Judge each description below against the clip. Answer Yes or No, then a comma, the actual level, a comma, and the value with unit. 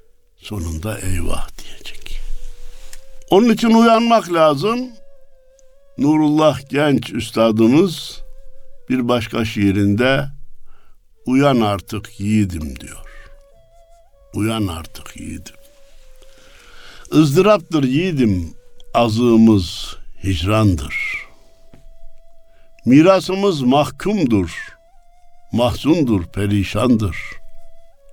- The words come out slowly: Yes, slow, 60 wpm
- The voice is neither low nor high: Yes, medium, 145 Hz